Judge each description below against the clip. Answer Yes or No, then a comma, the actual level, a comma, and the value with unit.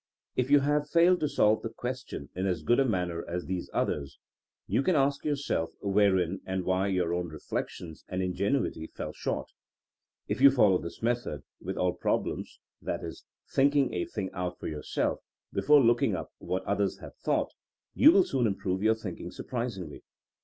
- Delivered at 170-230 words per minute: Yes, average, 185 wpm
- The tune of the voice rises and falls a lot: Yes, wide, 6.9 semitones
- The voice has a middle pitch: No, low, 100 Hz